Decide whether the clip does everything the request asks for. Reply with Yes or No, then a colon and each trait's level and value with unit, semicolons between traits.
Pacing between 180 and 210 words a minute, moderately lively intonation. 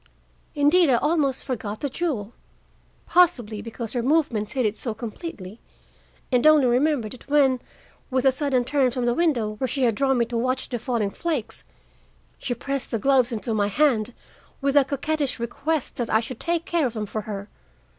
Yes: average, 185 wpm; average, 4.0 semitones